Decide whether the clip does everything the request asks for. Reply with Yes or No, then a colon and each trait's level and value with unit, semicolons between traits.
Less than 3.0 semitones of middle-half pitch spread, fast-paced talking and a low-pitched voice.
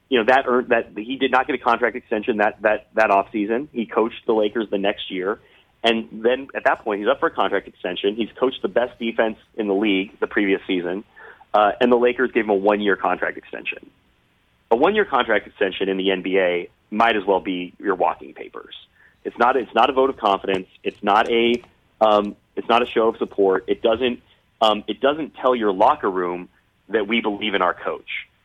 No: average, 3.3 semitones; fast, 215 wpm; low, 110 Hz